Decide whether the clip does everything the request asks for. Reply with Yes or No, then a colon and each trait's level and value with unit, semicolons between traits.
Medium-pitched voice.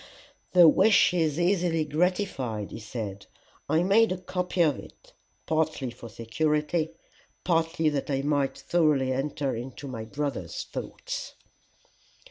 Yes: medium, 155 Hz